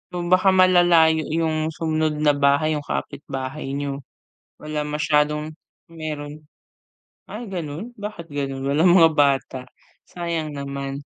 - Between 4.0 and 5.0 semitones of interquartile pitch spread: No, narrow, 2.4 semitones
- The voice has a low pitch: No, medium, 150 Hz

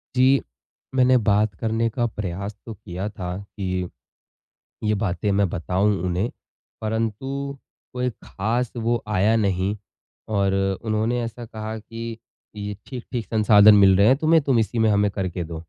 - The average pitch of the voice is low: Yes, low, 110 Hz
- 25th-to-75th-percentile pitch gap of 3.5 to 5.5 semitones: No, average, 2.8 semitones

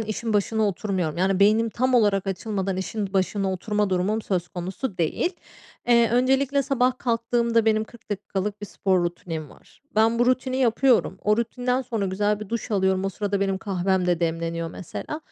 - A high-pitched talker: Yes, high, 210 Hz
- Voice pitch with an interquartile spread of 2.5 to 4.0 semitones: Yes, average, 3.6 semitones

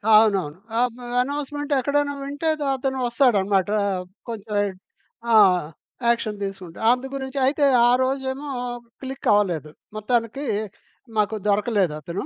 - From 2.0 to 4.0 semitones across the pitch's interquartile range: No, average, 5.0 semitones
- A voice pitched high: Yes, high, 235 Hz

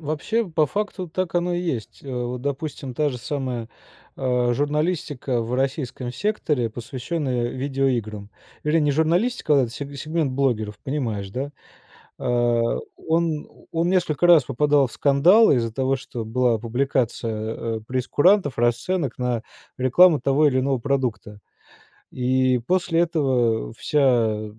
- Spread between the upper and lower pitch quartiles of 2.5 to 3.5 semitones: No, average, 4.3 semitones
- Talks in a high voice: No, low, 135 Hz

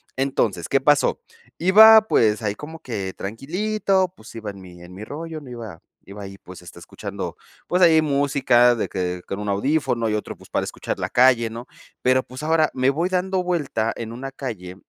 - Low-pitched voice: Yes, low, 125 Hz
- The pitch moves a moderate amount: No, wide, 7.0 semitones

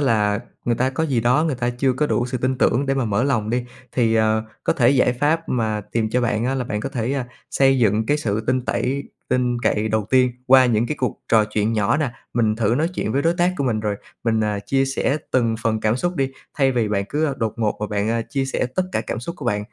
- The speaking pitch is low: Yes, low, 120 Hz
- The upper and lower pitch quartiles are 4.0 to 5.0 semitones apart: No, average, 3.4 semitones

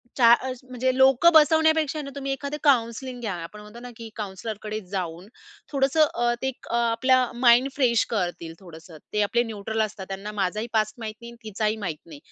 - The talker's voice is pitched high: Yes, high, 235 Hz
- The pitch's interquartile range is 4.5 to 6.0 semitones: No, average, 3.9 semitones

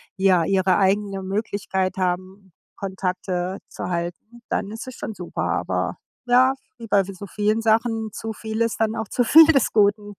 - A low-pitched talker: No, high, 205 Hz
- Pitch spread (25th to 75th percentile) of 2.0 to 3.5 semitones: Yes, average, 2.9 semitones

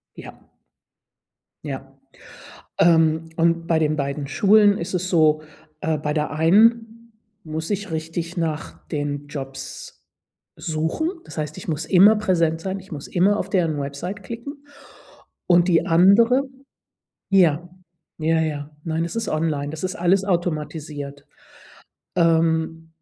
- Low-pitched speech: No, medium, 165 Hz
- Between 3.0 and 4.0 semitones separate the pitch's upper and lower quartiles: Yes, average, 3.3 semitones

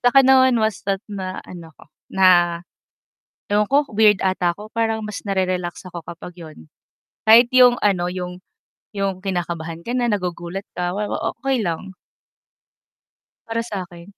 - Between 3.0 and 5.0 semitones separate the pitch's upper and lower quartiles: Yes, average, 3.9 semitones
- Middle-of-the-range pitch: No, high, 195 Hz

